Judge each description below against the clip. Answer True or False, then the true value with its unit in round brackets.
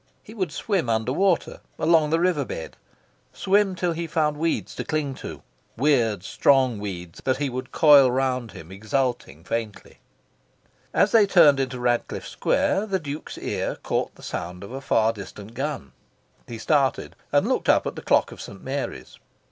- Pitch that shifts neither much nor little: False (5.7 semitones)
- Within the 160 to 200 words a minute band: True (170 wpm)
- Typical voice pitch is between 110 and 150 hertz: True (135 Hz)